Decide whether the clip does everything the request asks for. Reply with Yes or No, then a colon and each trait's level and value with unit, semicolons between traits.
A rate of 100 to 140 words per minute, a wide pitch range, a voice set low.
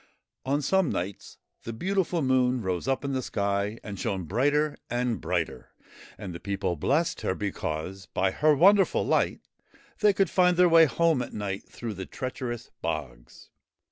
No: average, 165 wpm; wide, 7.9 semitones; low, 120 Hz